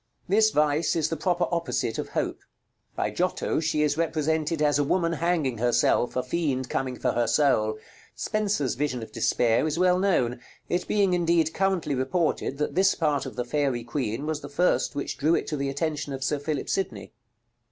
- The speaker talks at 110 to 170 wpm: No, average, 190 wpm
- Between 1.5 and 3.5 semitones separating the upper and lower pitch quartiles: No, average, 4.2 semitones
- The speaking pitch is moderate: Yes, medium, 150 Hz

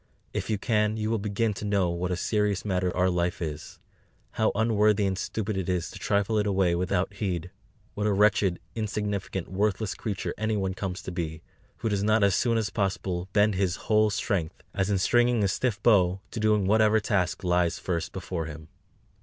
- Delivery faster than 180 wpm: Yes, average, 195 wpm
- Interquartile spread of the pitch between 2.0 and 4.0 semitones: Yes, average, 2.8 semitones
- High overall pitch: No, low, 100 Hz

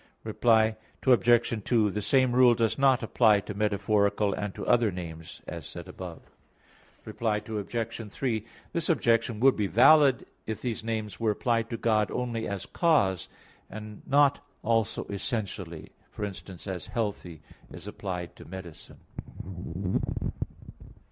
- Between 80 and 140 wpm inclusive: Yes, slow, 135 wpm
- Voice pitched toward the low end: Yes, low, 110 Hz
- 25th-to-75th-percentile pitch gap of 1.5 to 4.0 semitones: Yes, average, 2.9 semitones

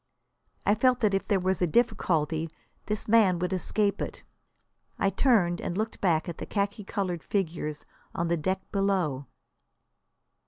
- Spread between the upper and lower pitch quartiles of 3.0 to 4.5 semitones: Yes, average, 3.3 semitones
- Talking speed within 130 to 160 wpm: Yes, average, 155 wpm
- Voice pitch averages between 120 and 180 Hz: No, high, 190 Hz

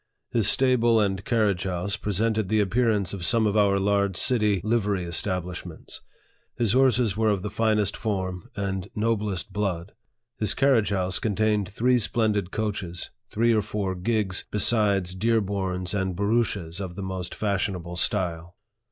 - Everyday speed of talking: Yes, average, 150 wpm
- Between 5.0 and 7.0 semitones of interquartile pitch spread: No, average, 2.8 semitones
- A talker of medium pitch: No, low, 100 Hz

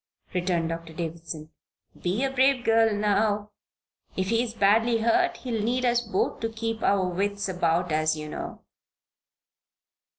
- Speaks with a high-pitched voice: Yes, high, 205 Hz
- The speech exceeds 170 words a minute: No, average, 145 wpm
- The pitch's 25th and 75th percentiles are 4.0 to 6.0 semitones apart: Yes, average, 4.7 semitones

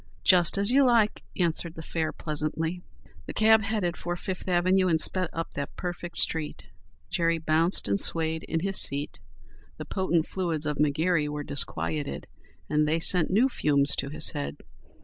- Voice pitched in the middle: Yes, medium, 165 Hz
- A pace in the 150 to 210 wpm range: Yes, average, 170 wpm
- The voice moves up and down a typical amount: Yes, average, 3.3 semitones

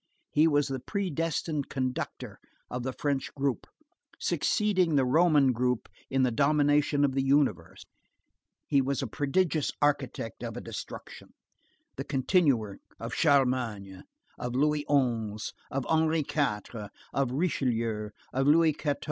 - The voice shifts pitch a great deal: No, average, 3.2 semitones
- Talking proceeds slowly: Yes, slow, 130 wpm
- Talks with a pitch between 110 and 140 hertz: Yes, low, 135 Hz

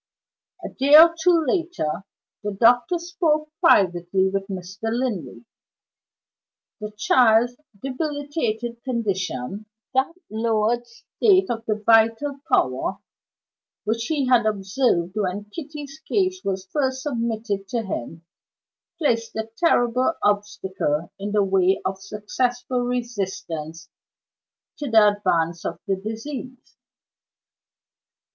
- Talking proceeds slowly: Yes, slow, 110 wpm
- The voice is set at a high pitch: Yes, high, 225 Hz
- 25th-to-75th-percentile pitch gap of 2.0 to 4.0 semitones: No, average, 5.2 semitones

